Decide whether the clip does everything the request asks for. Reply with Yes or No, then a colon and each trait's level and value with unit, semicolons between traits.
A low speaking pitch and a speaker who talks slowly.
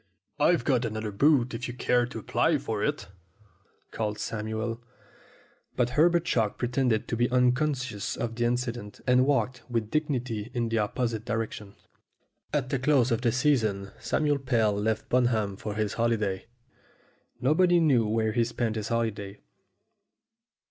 No: low, 120 Hz; average, 150 wpm